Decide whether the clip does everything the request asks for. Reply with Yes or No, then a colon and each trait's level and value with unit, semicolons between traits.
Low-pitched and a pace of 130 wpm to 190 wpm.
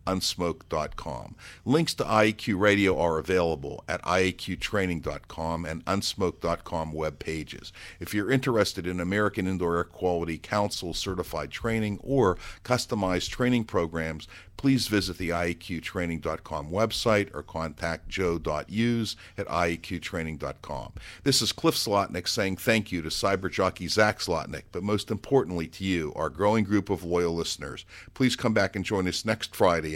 Yes: very low, 95 Hz; average, 140 wpm